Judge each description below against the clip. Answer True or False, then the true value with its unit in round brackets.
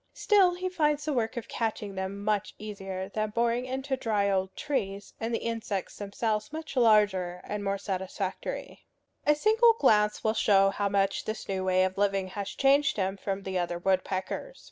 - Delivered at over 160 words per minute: True (180 wpm)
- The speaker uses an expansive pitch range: False (4.1 semitones)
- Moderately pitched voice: False (210 Hz)